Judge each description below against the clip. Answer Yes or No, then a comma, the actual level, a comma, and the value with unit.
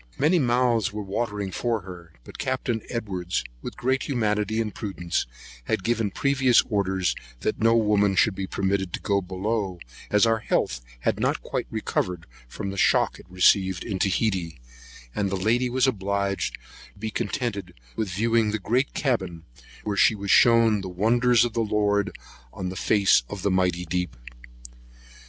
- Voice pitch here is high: No, low, 105 Hz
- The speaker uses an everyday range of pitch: Yes, average, 3.4 semitones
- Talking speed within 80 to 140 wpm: No, average, 165 wpm